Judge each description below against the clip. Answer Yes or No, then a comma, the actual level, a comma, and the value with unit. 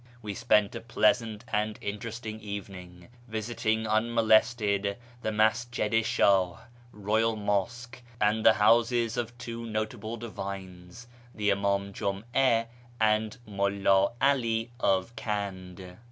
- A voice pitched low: Yes, low, 110 Hz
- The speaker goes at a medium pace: No, slow, 110 wpm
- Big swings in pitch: No, narrow, 2.5 semitones